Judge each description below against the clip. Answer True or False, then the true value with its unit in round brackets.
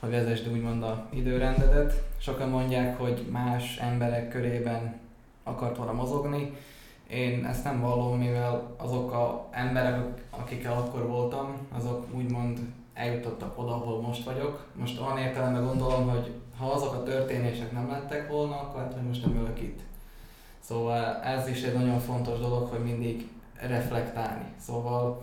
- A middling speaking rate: True (145 wpm)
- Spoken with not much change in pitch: True (1.3 semitones)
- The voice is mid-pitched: False (120 Hz)